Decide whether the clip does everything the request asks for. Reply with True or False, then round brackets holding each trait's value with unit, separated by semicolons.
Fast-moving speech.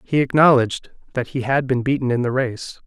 True (210 wpm)